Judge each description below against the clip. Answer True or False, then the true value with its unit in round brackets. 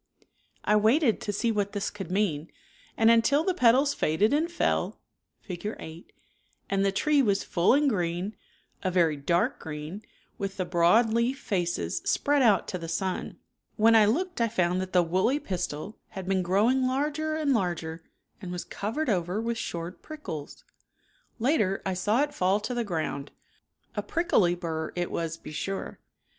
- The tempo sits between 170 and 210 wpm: True (175 wpm)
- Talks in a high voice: True (200 Hz)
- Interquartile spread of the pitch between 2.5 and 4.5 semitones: False (5.4 semitones)